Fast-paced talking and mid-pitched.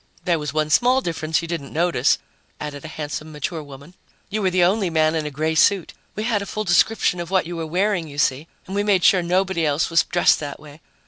Yes: fast, 240 wpm; medium, 165 Hz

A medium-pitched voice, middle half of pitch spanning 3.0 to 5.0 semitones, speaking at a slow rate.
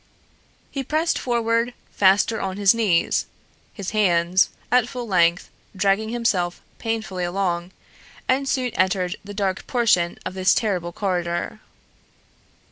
No: high, 195 Hz; average, 4.2 semitones; slow, 125 wpm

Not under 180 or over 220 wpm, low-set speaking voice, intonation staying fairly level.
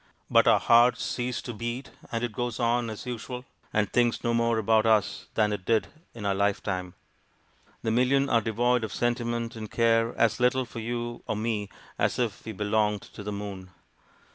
Yes: average, 190 wpm; low, 115 Hz; narrow, 2.3 semitones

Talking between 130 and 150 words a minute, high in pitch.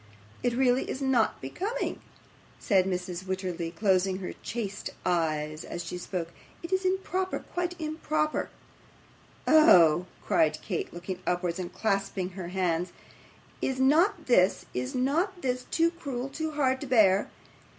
Yes: average, 140 wpm; high, 205 Hz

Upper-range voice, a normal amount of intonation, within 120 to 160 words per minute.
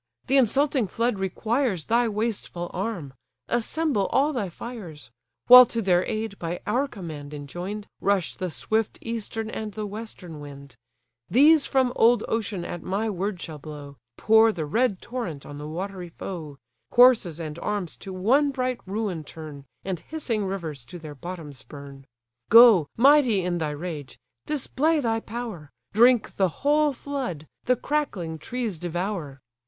No: high, 200 Hz; wide, 6.5 semitones; average, 150 wpm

